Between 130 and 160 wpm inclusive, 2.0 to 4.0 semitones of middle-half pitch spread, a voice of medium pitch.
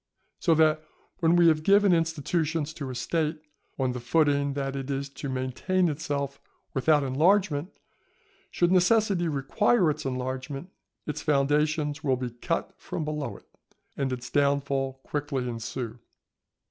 Yes: average, 140 wpm; average, 3.3 semitones; medium, 145 Hz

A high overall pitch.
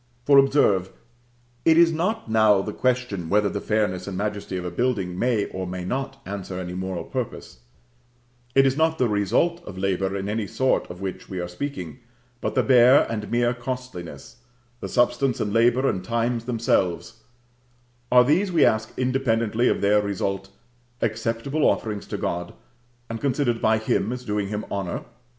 No: low, 110 Hz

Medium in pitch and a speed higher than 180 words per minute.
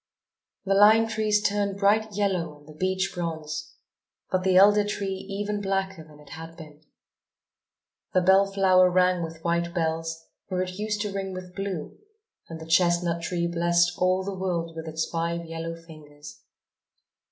No: medium, 180 Hz; average, 165 wpm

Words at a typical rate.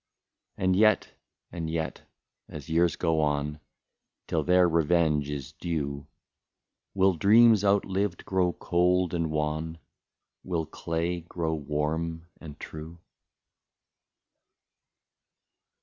No: slow, 100 wpm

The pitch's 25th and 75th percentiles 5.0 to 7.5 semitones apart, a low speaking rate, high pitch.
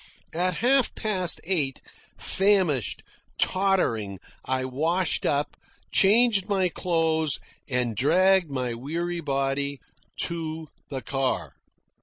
No: wide, 5.4 semitones; slow, 100 wpm; medium, 160 Hz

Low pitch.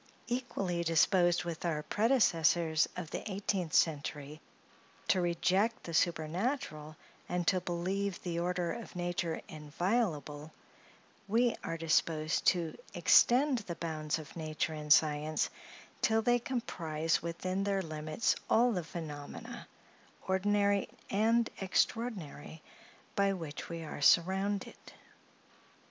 No: medium, 175 Hz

